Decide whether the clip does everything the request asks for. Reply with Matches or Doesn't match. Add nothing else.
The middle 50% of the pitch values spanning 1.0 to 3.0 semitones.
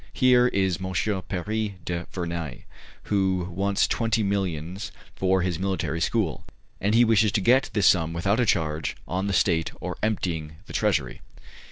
Doesn't match